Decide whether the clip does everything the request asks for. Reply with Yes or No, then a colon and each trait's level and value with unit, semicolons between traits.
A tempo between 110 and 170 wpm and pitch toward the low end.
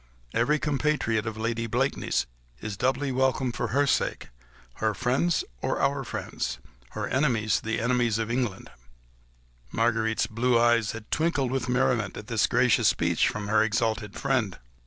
Yes: average, 150 wpm; low, 120 Hz